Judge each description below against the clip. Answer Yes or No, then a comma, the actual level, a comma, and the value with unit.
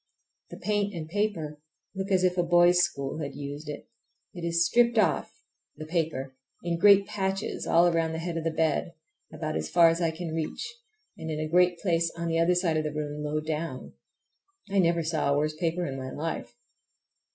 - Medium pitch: Yes, medium, 165 Hz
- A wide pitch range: No, narrow, 2.6 semitones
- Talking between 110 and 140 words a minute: No, average, 195 wpm